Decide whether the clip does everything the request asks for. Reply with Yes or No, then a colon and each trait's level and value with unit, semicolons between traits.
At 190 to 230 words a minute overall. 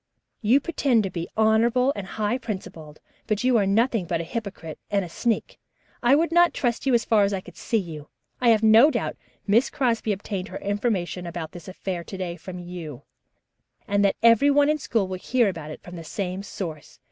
Yes: fast, 205 wpm